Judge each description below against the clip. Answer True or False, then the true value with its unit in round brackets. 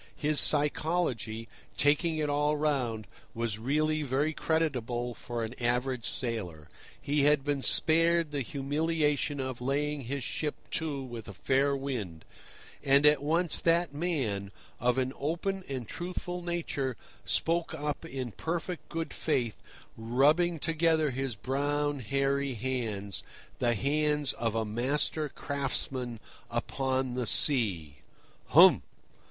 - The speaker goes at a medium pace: False (125 wpm)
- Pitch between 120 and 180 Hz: True (140 Hz)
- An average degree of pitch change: True (4.0 semitones)